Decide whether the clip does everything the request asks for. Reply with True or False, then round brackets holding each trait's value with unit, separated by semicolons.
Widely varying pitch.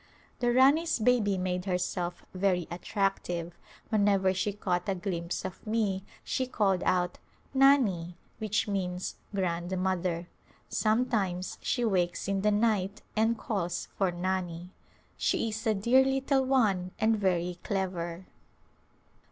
False (3.4 semitones)